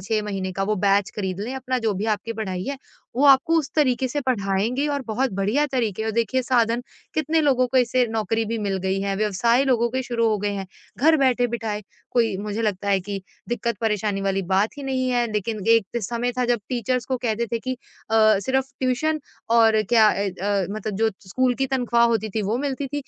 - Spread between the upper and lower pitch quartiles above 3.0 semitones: Yes, average, 3.7 semitones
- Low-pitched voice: No, high, 230 Hz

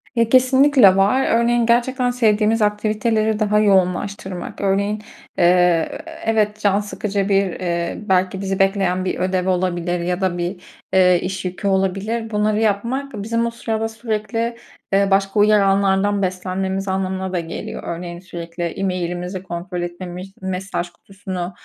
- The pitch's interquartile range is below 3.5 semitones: Yes, average, 2.8 semitones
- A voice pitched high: Yes, high, 195 Hz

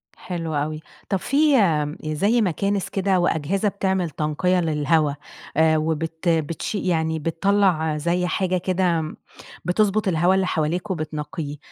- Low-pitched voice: No, medium, 170 Hz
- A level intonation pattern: No, average, 3.5 semitones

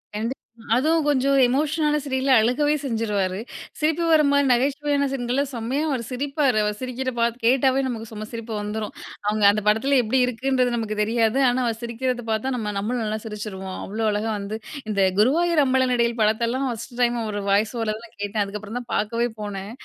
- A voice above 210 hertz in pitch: Yes, high, 235 Hz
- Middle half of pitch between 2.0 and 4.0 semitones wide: Yes, average, 3.7 semitones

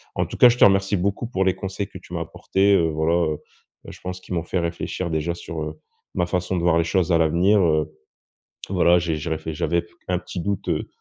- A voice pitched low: Yes, very low, 85 Hz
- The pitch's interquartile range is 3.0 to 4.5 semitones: No, narrow, 2.5 semitones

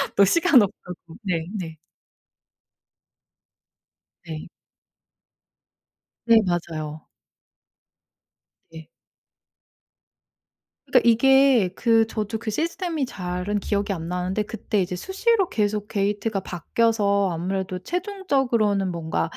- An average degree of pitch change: Yes, average, 4.4 semitones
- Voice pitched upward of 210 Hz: No, high, 205 Hz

